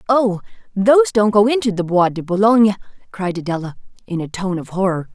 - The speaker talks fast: No, average, 185 wpm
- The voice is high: Yes, high, 200 Hz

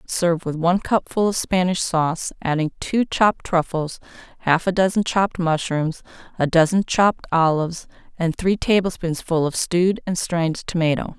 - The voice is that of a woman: Yes, female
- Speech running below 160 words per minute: Yes, average, 150 wpm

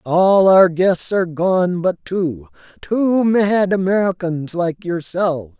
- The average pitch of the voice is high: No, medium, 180 Hz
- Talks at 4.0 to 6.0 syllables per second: No, 3.5 syllables/s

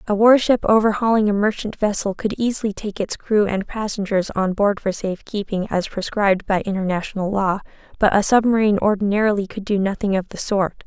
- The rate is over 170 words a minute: Yes, average, 180 wpm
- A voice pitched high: Yes, high, 205 Hz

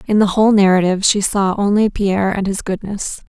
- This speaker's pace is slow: No, average, 200 wpm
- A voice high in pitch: Yes, high, 200 Hz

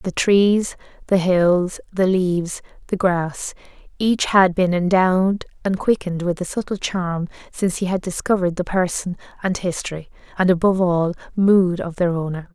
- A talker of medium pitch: Yes, medium, 180 Hz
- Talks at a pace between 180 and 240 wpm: No, average, 155 wpm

